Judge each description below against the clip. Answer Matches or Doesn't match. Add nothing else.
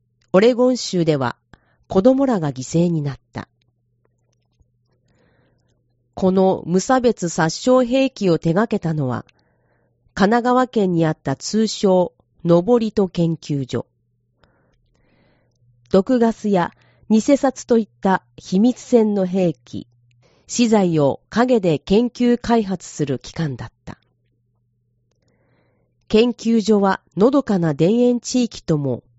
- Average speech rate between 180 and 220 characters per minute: Matches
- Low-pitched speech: Doesn't match